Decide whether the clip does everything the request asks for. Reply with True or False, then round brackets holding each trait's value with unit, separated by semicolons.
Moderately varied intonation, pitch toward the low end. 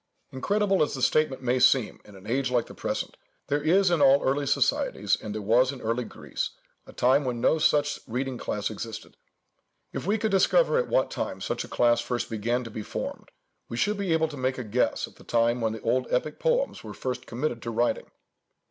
True (4.6 semitones; 130 Hz)